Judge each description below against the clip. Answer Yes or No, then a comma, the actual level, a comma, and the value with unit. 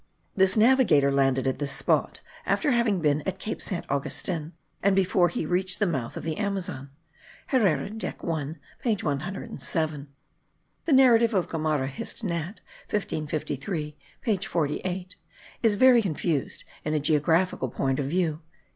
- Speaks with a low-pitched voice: No, medium, 170 Hz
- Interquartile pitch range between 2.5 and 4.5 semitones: No, average, 5.1 semitones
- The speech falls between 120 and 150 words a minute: Yes, average, 145 wpm